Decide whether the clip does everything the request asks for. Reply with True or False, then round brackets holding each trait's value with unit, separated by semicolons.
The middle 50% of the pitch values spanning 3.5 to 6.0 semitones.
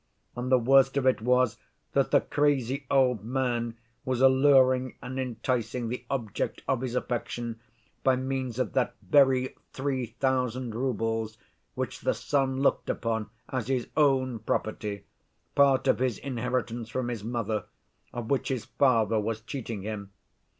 False (2.5 semitones)